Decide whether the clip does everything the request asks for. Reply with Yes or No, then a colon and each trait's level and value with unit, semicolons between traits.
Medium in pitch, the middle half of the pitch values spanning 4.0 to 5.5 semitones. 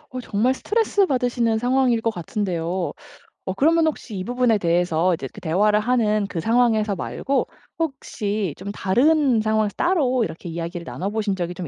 No: high, 215 Hz; average, 5.2 semitones